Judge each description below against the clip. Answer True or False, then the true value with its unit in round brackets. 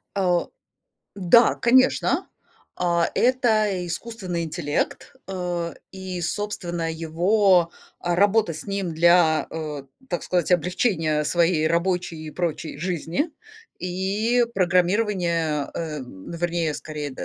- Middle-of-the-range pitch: True (175 Hz)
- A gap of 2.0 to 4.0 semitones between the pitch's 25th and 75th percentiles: True (2.9 semitones)